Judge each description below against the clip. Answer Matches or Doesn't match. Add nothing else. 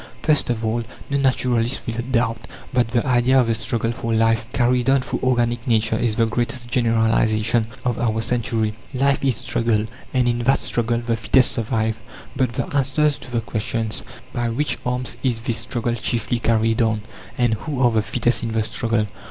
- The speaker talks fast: Doesn't match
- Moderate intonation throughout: Doesn't match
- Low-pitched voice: Matches